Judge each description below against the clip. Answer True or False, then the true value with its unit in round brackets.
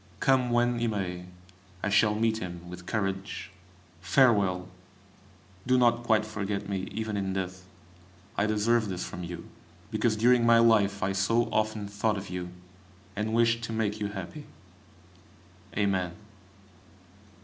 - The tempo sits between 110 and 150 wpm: True (140 wpm)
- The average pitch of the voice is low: True (105 Hz)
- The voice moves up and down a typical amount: True (3.2 semitones)